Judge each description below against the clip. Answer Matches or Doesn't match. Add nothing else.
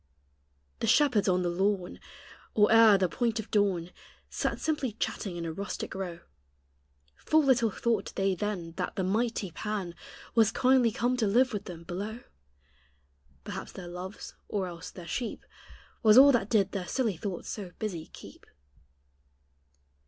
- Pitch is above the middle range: Matches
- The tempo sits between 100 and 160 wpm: Matches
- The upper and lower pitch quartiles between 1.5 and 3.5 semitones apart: Doesn't match